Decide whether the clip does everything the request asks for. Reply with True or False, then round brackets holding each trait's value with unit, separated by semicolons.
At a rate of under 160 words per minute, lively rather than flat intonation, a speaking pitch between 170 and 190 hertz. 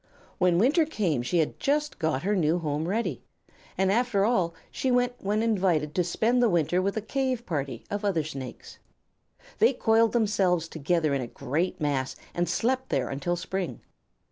False (175 wpm; 6.1 semitones; 185 Hz)